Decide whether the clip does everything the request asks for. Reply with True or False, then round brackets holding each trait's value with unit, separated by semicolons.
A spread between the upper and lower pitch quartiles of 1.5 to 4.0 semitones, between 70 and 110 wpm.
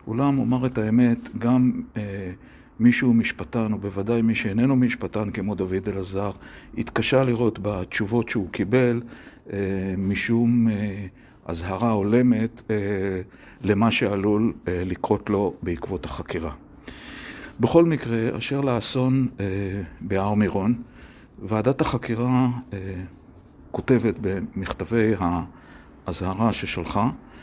True (3.7 semitones; 105 wpm)